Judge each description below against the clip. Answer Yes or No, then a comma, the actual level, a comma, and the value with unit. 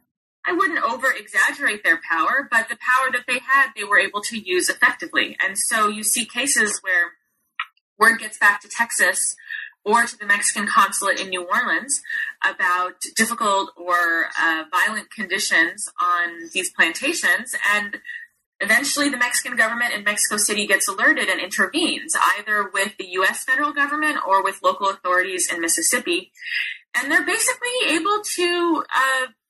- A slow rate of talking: No, average, 155 wpm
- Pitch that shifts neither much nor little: No, wide, 8.1 semitones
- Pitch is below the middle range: No, high, 245 Hz